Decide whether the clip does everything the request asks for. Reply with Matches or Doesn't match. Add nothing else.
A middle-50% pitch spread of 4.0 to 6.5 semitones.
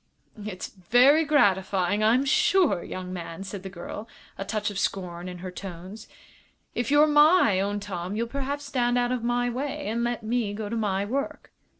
Matches